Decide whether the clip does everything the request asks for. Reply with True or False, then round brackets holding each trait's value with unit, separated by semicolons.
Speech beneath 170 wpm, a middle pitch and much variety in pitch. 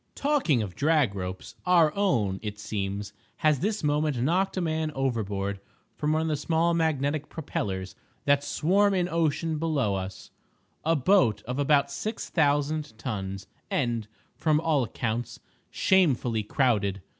True (135 wpm; 145 Hz; 7.0 semitones)